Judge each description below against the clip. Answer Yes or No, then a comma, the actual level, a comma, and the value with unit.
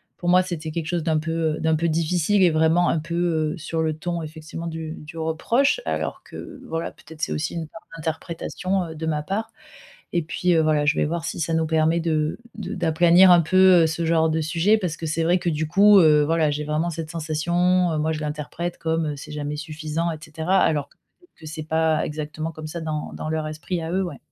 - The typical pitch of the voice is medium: Yes, medium, 160 Hz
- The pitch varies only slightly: Yes, narrow, 1.7 semitones